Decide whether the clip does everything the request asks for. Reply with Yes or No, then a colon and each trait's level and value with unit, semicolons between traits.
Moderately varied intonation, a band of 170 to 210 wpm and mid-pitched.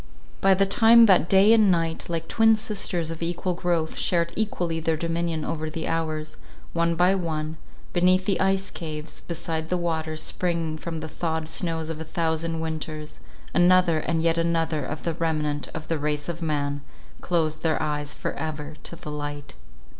No: narrow, 1.9 semitones; average, 175 wpm; medium, 165 Hz